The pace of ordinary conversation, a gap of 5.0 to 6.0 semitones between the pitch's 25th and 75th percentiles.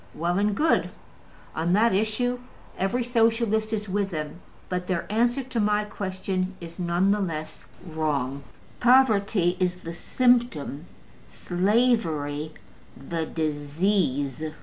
No: slow, 120 wpm; average, 5.3 semitones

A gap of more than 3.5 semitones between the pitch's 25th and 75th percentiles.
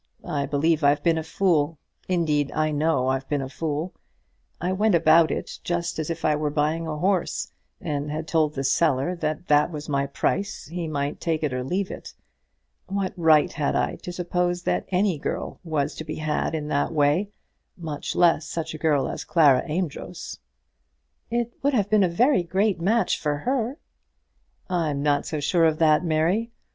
No: average, 3.2 semitones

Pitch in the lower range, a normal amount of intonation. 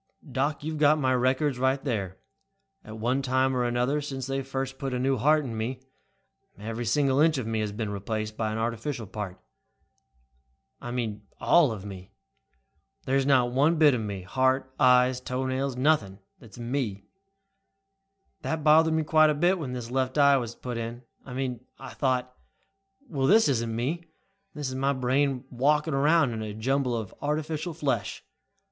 Yes: low, 130 Hz; average, 3.5 semitones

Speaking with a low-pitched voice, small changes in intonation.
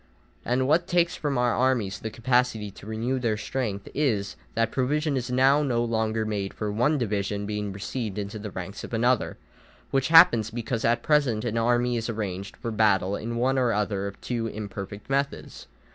No: low, 115 Hz; average, 3.5 semitones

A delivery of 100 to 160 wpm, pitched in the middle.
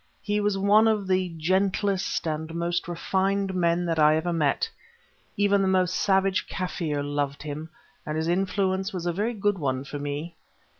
No: average, 170 wpm; medium, 180 Hz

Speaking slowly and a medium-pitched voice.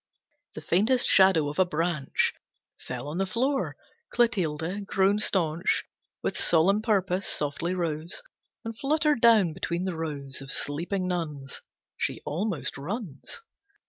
Yes: slow, 130 wpm; medium, 180 Hz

